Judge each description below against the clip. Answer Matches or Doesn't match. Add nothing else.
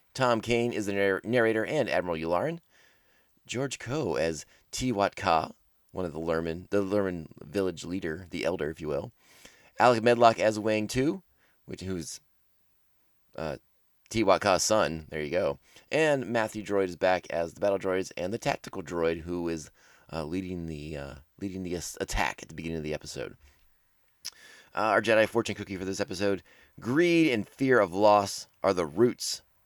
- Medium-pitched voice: Doesn't match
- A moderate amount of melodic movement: Matches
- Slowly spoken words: Doesn't match